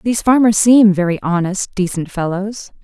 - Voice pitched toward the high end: Yes, high, 200 Hz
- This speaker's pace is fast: No, average, 150 wpm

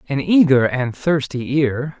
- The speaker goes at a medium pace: Yes, average, 150 wpm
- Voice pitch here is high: No, low, 135 Hz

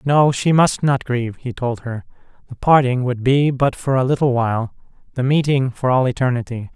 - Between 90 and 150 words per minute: No, average, 195 wpm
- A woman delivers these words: No, male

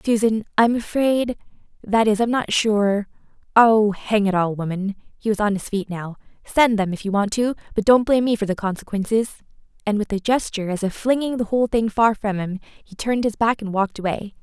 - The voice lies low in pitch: No, high, 215 Hz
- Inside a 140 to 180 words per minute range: No, average, 195 wpm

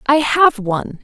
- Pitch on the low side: No, very high, 250 Hz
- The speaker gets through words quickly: No, average, 175 wpm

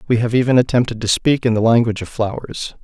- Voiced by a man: Yes, male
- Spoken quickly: Yes, fast, 235 wpm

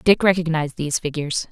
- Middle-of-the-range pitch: Yes, medium, 160 Hz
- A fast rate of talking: No, average, 160 wpm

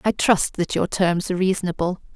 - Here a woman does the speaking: Yes, female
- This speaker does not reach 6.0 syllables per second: Yes, 5.6 syllables/s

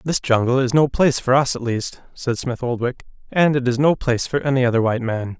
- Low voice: Yes, low, 130 Hz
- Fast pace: Yes, fast, 245 wpm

